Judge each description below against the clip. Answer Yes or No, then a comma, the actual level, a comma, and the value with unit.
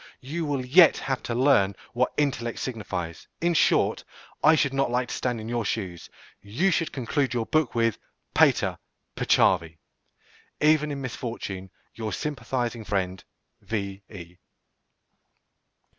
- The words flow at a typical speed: No, slow, 130 wpm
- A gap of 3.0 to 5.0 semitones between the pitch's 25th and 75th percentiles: No, wide, 5.6 semitones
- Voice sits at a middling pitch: No, low, 120 Hz